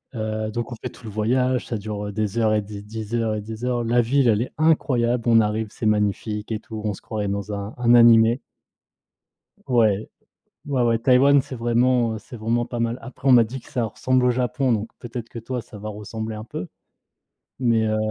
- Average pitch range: No, narrow, 2.2 semitones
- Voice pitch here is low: Yes, low, 115 Hz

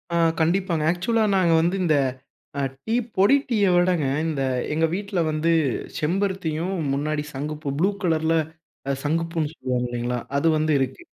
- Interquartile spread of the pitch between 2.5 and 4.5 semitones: Yes, average, 3.5 semitones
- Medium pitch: Yes, medium, 165 Hz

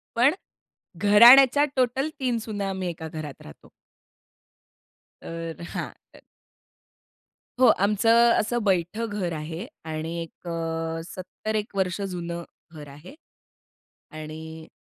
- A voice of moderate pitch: Yes, medium, 180 Hz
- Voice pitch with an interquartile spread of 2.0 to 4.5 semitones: No, average, 5.3 semitones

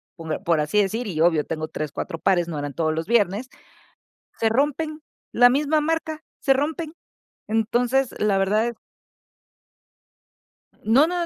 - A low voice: No, high, 225 Hz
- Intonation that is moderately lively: No, wide, 8.8 semitones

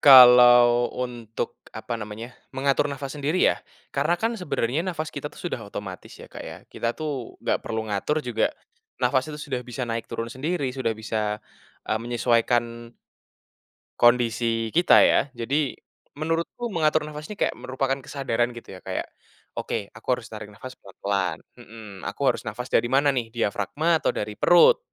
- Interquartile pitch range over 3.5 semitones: Yes, average, 4.1 semitones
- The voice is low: Yes, low, 125 Hz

